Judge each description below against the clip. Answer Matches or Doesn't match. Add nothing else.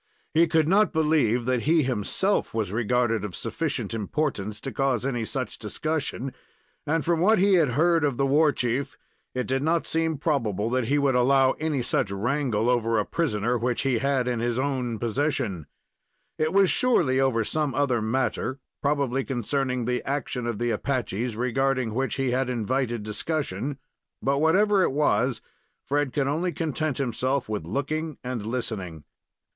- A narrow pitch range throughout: Doesn't match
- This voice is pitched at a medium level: Doesn't match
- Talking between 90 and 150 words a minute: Doesn't match